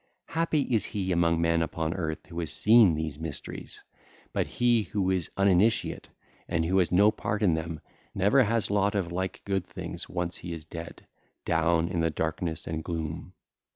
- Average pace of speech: Yes, average, 180 wpm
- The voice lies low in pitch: Yes, very low, 85 Hz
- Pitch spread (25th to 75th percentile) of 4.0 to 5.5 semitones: No, average, 3.6 semitones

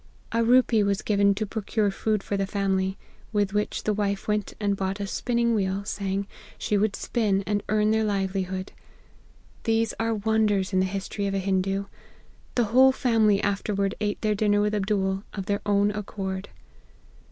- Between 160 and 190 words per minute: Yes, average, 175 wpm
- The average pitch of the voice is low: No, high, 205 Hz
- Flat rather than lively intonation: Yes, narrow, 1.6 semitones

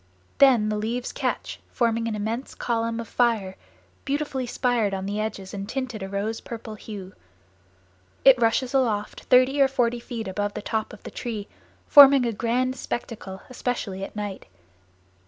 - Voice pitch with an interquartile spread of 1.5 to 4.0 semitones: Yes, average, 3.2 semitones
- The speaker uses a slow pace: No, average, 160 wpm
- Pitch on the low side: No, high, 230 Hz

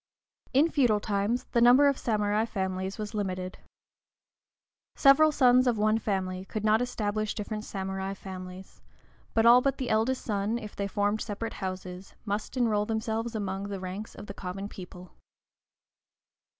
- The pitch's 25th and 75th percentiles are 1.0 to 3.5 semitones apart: Yes, average, 3.2 semitones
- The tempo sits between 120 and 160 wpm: Yes, average, 150 wpm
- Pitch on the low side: No, high, 210 Hz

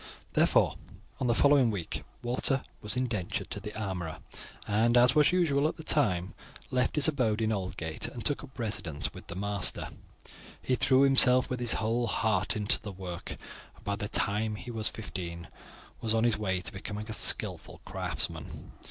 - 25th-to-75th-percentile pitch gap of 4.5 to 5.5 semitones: No, average, 3.9 semitones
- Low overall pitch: Yes, low, 110 Hz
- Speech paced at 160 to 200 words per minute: Yes, average, 180 wpm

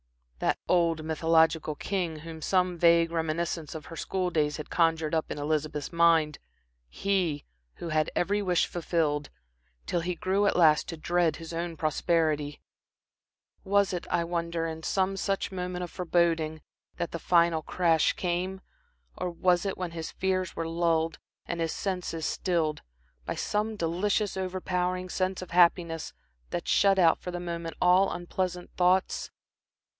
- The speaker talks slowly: No, average, 155 wpm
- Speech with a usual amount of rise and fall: No, narrow, 2.1 semitones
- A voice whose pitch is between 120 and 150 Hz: No, medium, 170 Hz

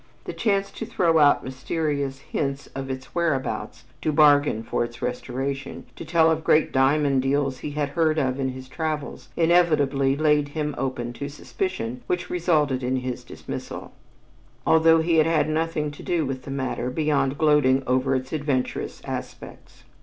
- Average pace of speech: Yes, average, 165 wpm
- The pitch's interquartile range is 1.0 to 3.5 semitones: Yes, average, 3.1 semitones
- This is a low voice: No, medium, 145 Hz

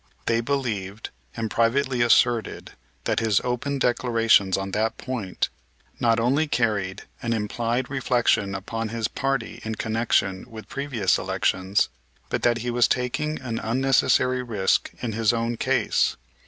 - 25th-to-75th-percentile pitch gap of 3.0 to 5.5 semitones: No, narrow, 2.4 semitones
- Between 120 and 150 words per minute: Yes, average, 140 wpm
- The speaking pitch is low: Yes, low, 115 Hz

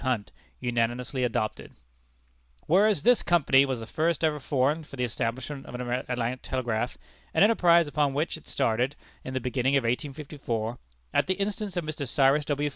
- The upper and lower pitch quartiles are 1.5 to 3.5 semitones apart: No, average, 3.9 semitones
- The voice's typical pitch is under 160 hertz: Yes, low, 135 Hz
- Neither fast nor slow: Yes, average, 170 wpm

